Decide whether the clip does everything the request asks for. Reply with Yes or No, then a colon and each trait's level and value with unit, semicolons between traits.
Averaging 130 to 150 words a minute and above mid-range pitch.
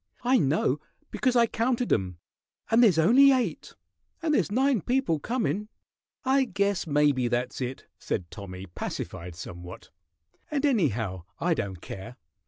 No: average, 140 wpm; medium, 165 Hz